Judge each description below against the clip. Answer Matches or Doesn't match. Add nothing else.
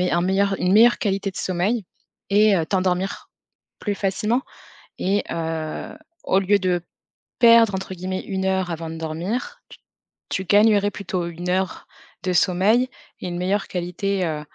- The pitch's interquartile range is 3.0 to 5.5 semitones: Doesn't match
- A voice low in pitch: Doesn't match